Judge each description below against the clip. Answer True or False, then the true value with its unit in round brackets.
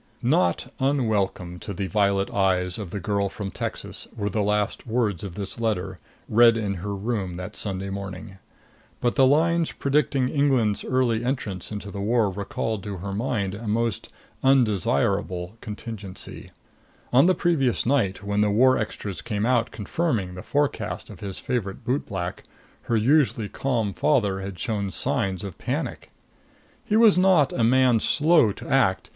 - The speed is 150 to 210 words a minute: True (160 wpm)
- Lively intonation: False (4.4 semitones)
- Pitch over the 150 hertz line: False (105 Hz)